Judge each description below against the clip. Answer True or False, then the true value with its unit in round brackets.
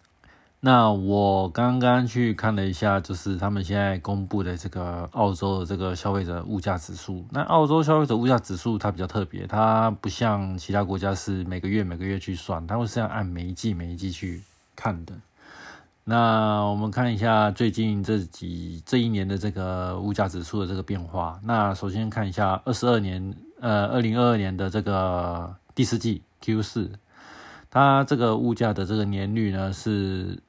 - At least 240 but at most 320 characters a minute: True (275 characters per minute)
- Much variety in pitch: False (2.9 semitones)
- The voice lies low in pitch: True (100 Hz)